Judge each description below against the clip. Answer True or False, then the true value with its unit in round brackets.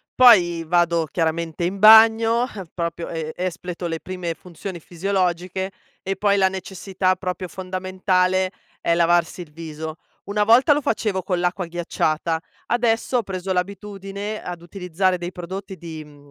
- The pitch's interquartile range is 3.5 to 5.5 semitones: False (2.6 semitones)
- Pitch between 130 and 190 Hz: True (185 Hz)